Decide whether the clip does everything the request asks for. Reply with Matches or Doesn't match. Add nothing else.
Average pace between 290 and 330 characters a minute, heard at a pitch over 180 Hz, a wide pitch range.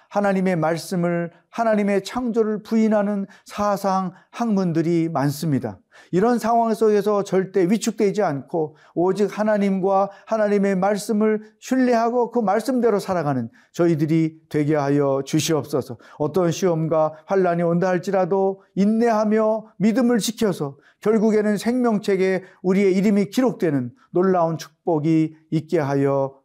Doesn't match